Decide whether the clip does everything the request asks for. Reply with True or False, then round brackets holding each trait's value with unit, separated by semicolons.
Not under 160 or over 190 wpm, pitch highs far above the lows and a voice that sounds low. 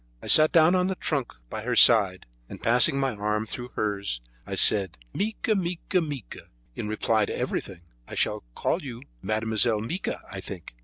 True (175 wpm; 6.7 semitones; 115 Hz)